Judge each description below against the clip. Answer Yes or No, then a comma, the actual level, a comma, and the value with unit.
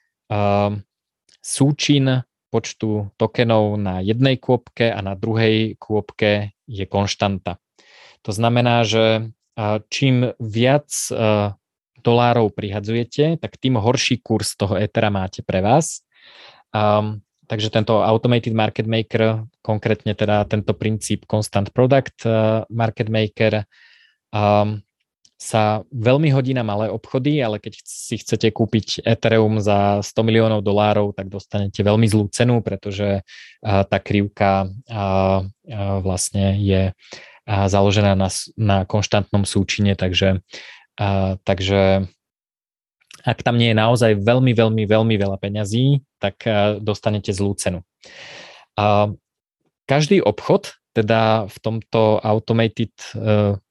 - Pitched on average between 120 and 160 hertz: No, low, 110 Hz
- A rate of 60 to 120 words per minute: Yes, average, 115 wpm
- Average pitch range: No, narrow, 2.0 semitones